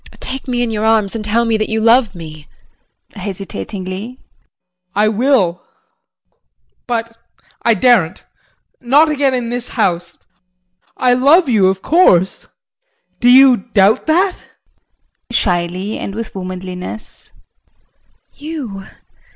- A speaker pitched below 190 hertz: No, high, 220 Hz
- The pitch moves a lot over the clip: No, average, 4.8 semitones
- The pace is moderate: No, slow, 120 wpm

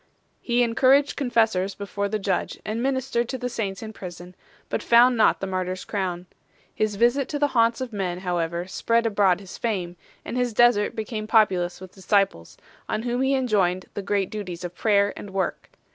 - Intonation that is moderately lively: Yes, average, 4.2 semitones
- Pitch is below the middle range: No, high, 210 Hz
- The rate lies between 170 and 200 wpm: Yes, average, 190 wpm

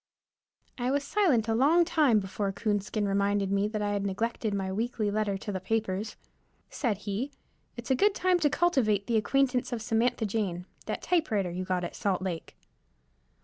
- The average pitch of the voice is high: Yes, high, 215 Hz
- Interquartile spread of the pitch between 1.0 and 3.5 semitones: No, average, 3.9 semitones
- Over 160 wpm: Yes, average, 180 wpm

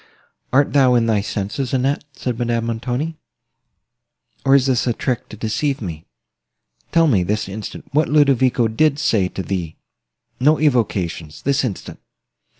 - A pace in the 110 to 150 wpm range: Yes, average, 140 wpm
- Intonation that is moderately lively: Yes, average, 4.7 semitones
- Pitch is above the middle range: No, low, 120 Hz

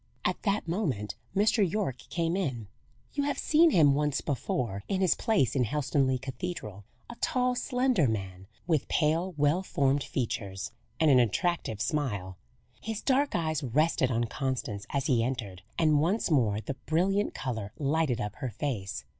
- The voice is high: No, medium, 145 Hz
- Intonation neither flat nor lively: No, wide, 7.2 semitones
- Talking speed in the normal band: Yes, average, 160 wpm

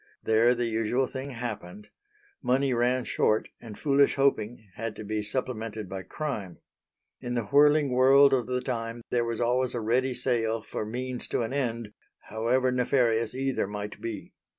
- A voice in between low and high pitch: No, low, 120 Hz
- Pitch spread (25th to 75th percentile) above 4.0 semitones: No, average, 2.7 semitones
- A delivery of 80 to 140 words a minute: No, average, 165 wpm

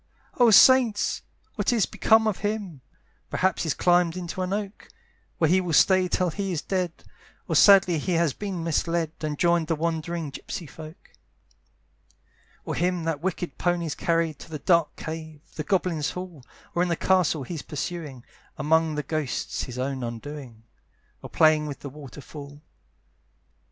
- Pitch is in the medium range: Yes, medium, 165 Hz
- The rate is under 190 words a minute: Yes, average, 160 wpm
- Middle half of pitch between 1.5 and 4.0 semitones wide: Yes, average, 3.3 semitones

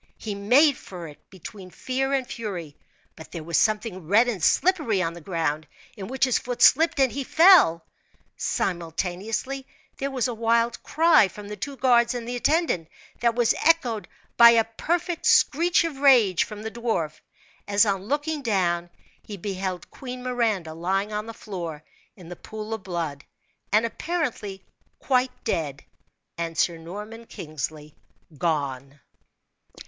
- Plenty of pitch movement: Yes, wide, 6.4 semitones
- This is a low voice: No, high, 215 Hz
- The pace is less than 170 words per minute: Yes, average, 155 wpm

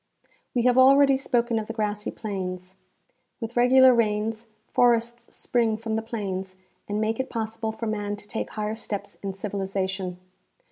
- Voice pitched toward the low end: No, high, 220 Hz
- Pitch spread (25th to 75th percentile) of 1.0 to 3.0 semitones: Yes, narrow, 2.4 semitones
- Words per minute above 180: No, average, 155 wpm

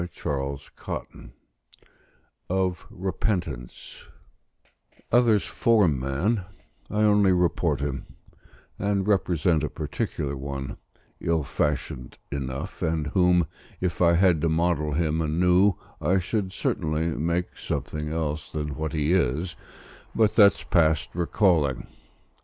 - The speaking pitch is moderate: No, very low, 85 Hz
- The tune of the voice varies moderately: Yes, average, 3.9 semitones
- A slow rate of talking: Yes, slow, 110 wpm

